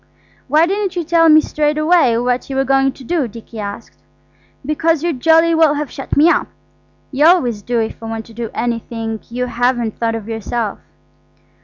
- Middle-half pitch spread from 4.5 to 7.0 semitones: Yes, wide, 5.4 semitones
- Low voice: No, very high, 260 Hz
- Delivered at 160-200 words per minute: Yes, average, 190 wpm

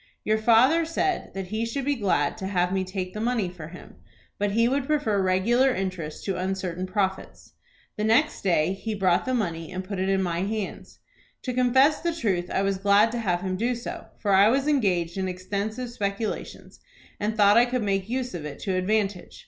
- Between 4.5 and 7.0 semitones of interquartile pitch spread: No, average, 4.1 semitones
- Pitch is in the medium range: No, high, 200 Hz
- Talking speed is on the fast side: Yes, fast, 210 wpm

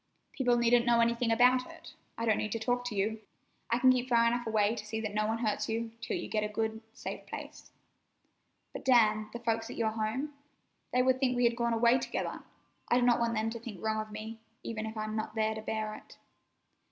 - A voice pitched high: Yes, high, 225 Hz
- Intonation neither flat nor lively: No, narrow, 1.8 semitones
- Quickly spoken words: Yes, fast, 235 wpm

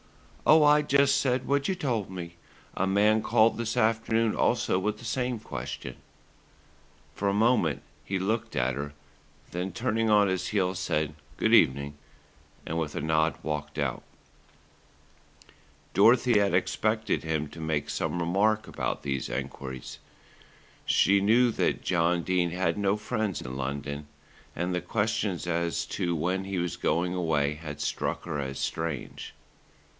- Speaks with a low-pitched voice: Yes, very low, 90 Hz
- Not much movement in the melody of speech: No, wide, 5.5 semitones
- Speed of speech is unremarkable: Yes, average, 150 wpm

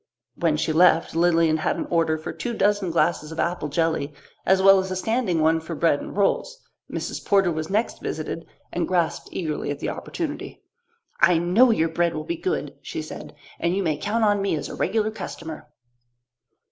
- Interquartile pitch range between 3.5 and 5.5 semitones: Yes, average, 3.8 semitones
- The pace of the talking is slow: No, average, 195 wpm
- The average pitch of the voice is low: No, medium, 170 Hz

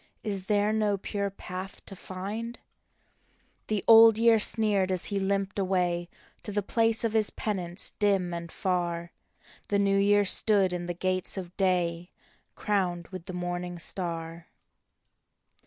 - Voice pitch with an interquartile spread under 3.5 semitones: Yes, average, 2.7 semitones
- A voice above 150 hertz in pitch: Yes, high, 190 Hz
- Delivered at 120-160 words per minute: Yes, average, 150 wpm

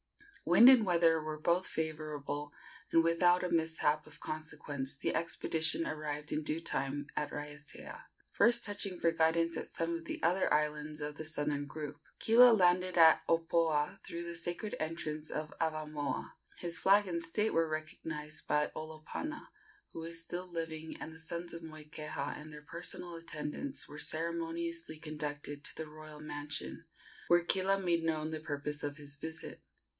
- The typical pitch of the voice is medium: Yes, medium, 160 Hz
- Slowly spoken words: No, average, 160 wpm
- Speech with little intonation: Yes, narrow, 2.0 semitones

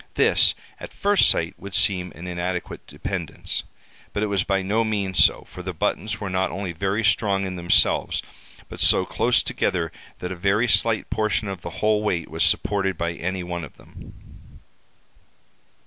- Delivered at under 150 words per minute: No, average, 175 wpm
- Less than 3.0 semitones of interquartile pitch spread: Yes, narrow, 2.6 semitones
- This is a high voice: No, very low, 95 Hz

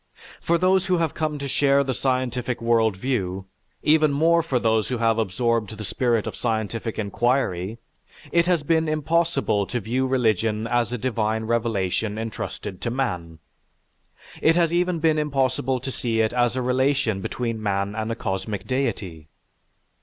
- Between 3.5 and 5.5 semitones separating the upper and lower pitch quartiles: Yes, average, 4.2 semitones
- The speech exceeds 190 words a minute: No, average, 160 wpm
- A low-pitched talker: Yes, low, 120 Hz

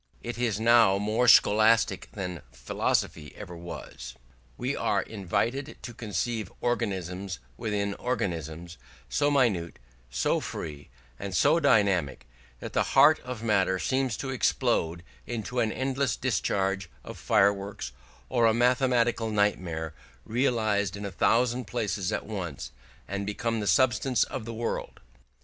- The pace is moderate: No, slow, 130 wpm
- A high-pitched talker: No, low, 105 Hz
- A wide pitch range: No, average, 4.4 semitones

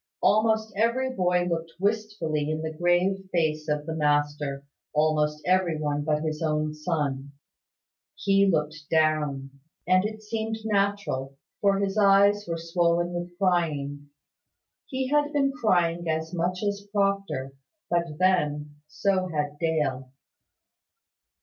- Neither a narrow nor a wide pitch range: Yes, average, 4.7 semitones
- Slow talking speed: Yes, slow, 130 wpm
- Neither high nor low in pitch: Yes, medium, 170 Hz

